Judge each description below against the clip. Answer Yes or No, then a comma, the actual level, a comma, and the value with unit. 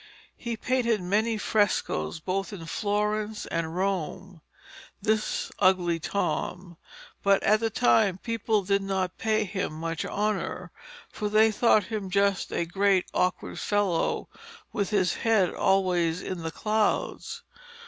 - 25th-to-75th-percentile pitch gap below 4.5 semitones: Yes, average, 2.8 semitones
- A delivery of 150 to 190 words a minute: No, slow, 135 wpm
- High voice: Yes, high, 200 Hz